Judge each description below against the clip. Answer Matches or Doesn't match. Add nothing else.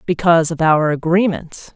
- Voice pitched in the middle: Matches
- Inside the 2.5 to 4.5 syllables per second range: Doesn't match